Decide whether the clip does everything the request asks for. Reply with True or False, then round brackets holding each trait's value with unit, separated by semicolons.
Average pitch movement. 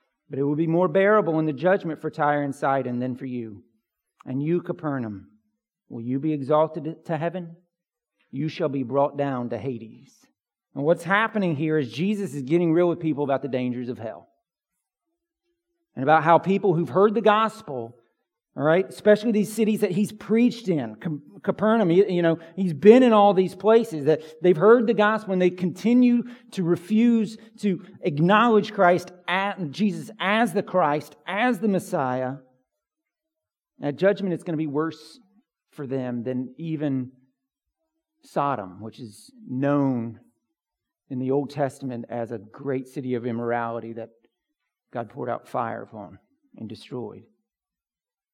False (7.2 semitones)